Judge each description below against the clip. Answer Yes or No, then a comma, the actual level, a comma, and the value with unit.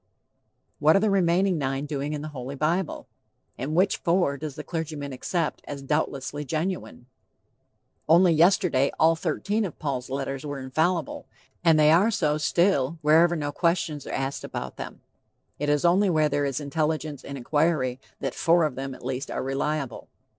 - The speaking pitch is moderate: Yes, medium, 150 Hz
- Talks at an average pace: Yes, average, 170 wpm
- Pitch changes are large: No, average, 3.4 semitones